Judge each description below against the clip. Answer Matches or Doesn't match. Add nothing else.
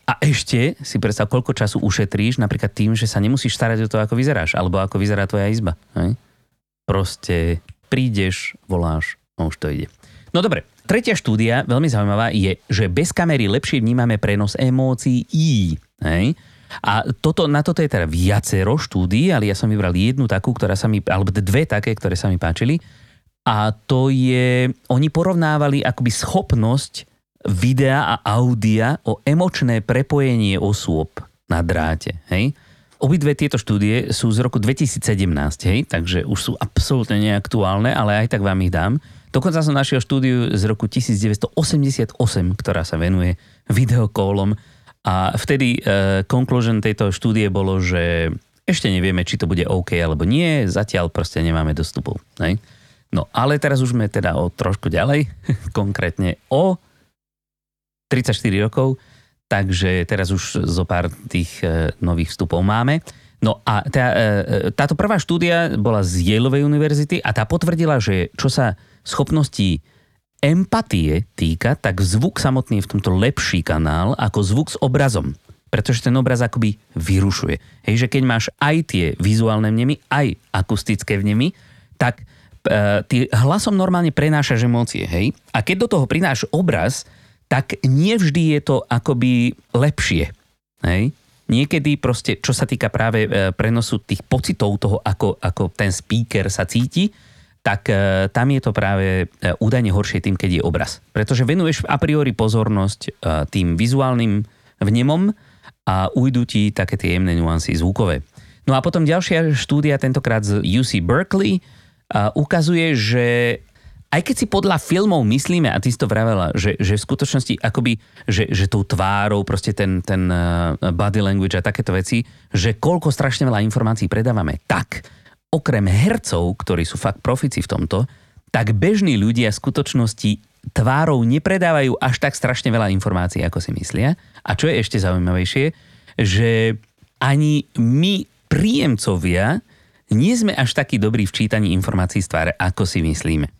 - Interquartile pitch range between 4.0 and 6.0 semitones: Matches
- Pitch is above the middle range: Doesn't match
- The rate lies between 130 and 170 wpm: Matches